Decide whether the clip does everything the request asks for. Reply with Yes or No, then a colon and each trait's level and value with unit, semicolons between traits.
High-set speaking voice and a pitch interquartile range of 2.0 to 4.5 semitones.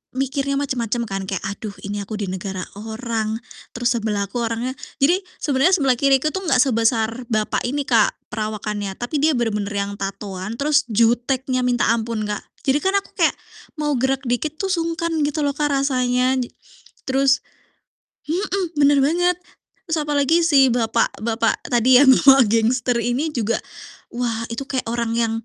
Yes: high, 245 Hz; average, 3.9 semitones